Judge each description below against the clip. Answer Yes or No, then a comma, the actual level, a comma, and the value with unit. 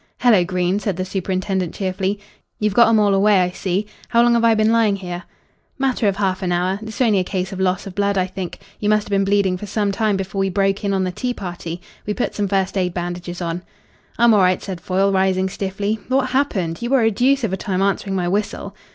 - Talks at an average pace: No, fast, 245 wpm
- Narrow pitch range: Yes, narrow, 2.3 semitones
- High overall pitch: Yes, high, 195 Hz